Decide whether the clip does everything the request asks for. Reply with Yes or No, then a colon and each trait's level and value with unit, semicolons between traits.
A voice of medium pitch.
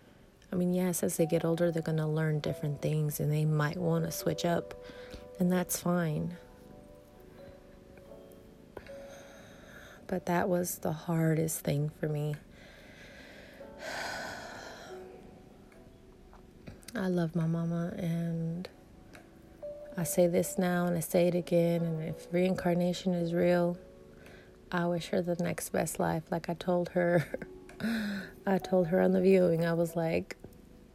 Yes: medium, 175 Hz